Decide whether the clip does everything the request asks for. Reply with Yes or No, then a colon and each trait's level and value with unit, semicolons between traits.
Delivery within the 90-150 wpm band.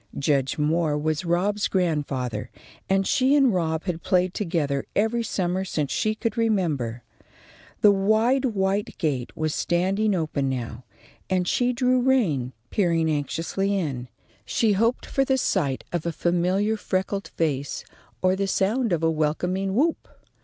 Yes: average, 145 wpm